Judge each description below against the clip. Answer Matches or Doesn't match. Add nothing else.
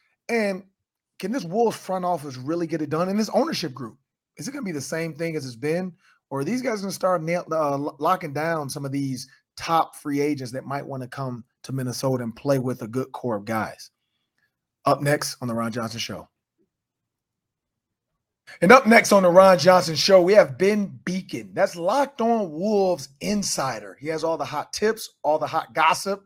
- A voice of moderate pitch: Matches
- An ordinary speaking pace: Doesn't match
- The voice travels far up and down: Matches